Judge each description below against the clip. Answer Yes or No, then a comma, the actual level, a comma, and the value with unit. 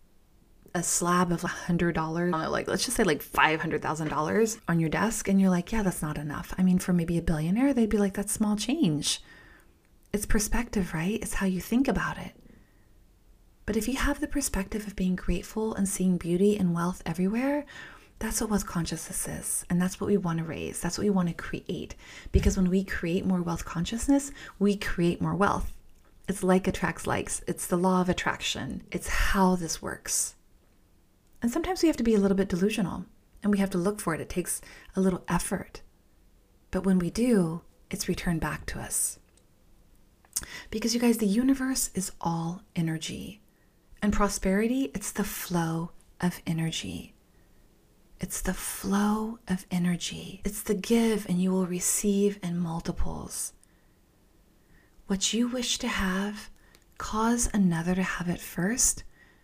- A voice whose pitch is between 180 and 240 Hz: Yes, high, 190 Hz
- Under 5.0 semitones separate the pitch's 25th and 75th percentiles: Yes, average, 3.5 semitones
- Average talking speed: Yes, average, 175 wpm